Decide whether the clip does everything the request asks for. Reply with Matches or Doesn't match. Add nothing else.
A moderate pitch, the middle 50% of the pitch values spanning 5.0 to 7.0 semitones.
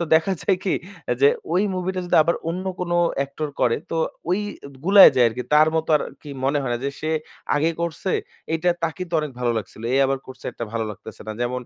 Matches